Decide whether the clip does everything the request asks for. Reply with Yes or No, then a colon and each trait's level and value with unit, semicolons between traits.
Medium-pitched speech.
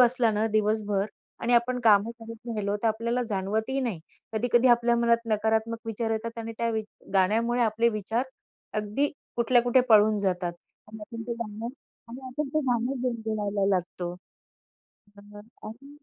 No: high, 225 Hz